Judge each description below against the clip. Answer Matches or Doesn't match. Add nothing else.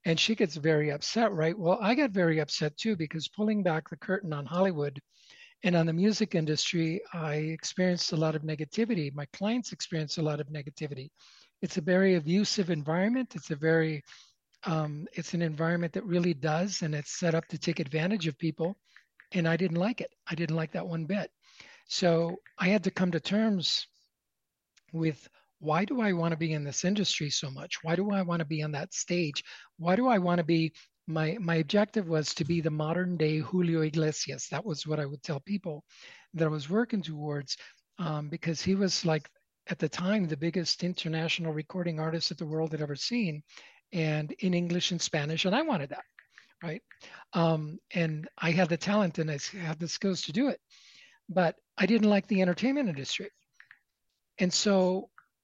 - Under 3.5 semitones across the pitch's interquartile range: Matches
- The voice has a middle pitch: Matches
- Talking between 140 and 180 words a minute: Doesn't match